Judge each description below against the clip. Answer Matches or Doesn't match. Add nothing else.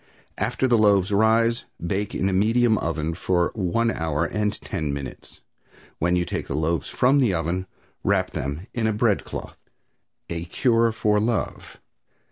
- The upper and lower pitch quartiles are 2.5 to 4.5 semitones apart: Doesn't match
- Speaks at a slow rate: Doesn't match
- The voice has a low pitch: Matches